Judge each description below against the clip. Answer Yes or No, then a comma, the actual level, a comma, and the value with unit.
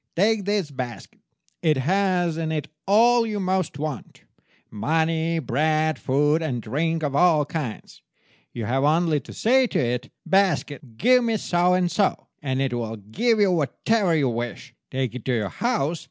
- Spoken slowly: No, average, 165 wpm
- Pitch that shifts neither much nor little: No, wide, 6.1 semitones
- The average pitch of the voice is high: No, medium, 160 Hz